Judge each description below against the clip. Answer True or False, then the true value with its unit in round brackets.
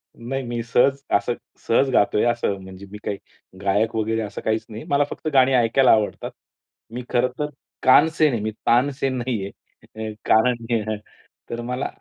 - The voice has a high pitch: False (120 Hz)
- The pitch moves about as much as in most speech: True (3.0 semitones)